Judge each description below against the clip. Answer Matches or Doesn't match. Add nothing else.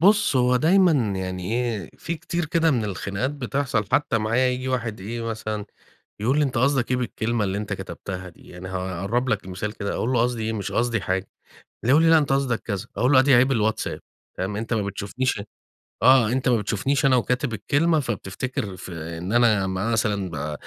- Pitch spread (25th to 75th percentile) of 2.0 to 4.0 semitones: Doesn't match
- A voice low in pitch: Matches